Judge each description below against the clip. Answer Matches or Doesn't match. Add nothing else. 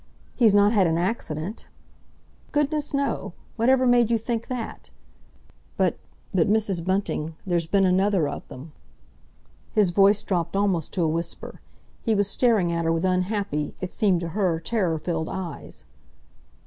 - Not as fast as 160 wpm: Matches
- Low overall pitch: Doesn't match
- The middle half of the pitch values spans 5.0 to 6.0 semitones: Doesn't match